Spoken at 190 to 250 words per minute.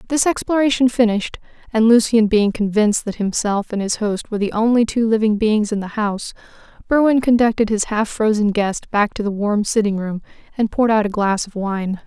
Yes: average, 200 wpm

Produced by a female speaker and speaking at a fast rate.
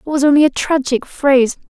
Yes: female; fast, 210 wpm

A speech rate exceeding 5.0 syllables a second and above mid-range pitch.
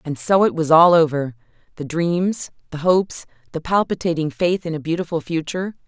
No: 5.5 syllables/s; medium, 160 Hz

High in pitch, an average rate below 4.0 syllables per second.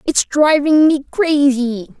Yes: very high, 280 Hz; 3.6 syllables/s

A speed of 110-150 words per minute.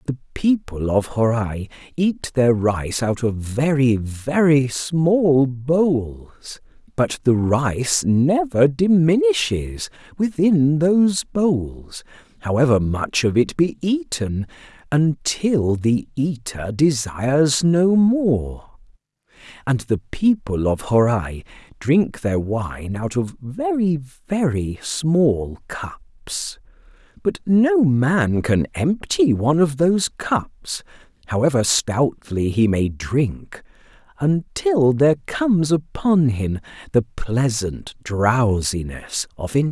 No: slow, 100 wpm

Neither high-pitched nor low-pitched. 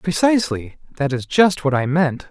Yes: medium, 155 Hz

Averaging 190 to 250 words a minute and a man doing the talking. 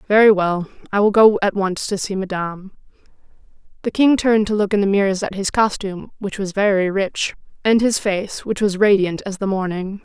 No: fast, 205 wpm; female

